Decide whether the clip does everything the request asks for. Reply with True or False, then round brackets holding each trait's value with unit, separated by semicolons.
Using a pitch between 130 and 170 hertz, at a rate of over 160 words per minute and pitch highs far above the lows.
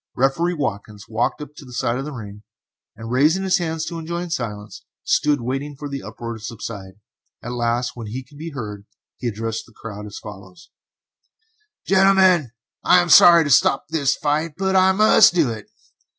True (135 Hz; 180 wpm; 6.4 semitones)